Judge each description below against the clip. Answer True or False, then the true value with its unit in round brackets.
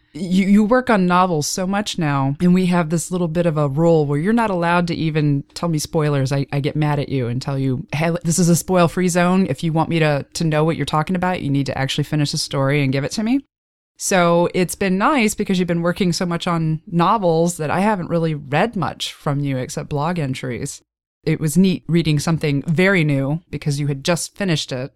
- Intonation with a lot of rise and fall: False (3.7 semitones)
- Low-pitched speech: False (165 Hz)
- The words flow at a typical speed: False (245 wpm)